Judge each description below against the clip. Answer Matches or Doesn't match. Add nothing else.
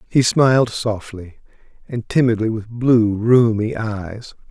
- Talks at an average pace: Doesn't match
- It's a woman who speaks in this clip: Doesn't match